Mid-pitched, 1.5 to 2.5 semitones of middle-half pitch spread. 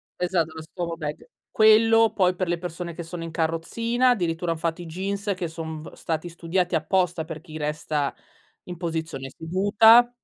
No: medium, 170 Hz; average, 2.9 semitones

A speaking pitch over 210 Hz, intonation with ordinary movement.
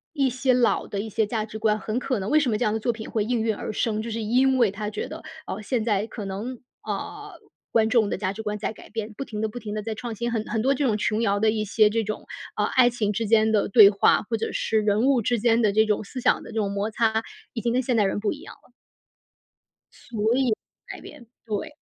No: high, 220 Hz; narrow, 2.2 semitones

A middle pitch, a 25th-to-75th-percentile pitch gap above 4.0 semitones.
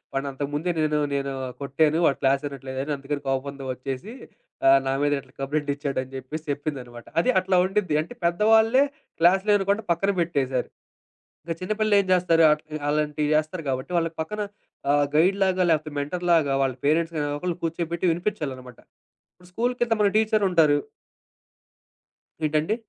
Yes: medium, 155 Hz; average, 4.5 semitones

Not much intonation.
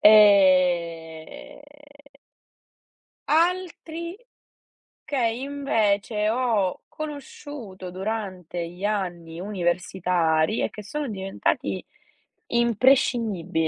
No: wide, 5.8 semitones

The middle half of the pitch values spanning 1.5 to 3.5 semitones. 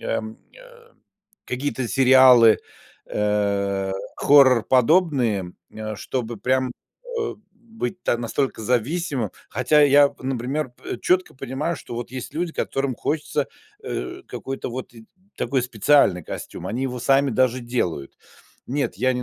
No: average, 3.9 semitones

